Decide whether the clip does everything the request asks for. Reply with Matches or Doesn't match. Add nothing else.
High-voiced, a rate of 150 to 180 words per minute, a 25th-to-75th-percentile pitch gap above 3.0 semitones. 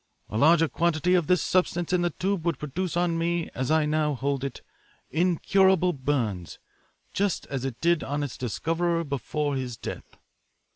Doesn't match